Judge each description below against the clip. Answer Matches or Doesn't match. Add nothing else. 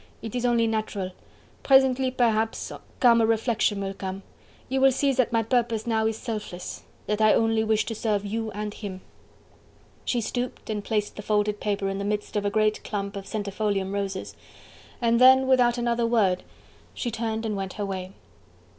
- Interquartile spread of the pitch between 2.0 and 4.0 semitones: Matches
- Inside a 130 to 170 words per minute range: Doesn't match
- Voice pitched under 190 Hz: Doesn't match